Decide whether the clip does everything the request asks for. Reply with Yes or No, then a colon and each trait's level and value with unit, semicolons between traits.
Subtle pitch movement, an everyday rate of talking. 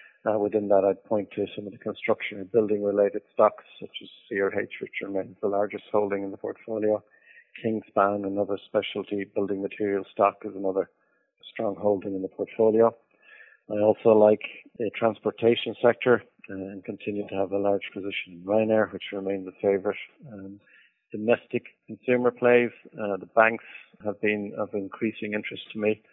Yes: narrow, 1.7 semitones; average, 170 wpm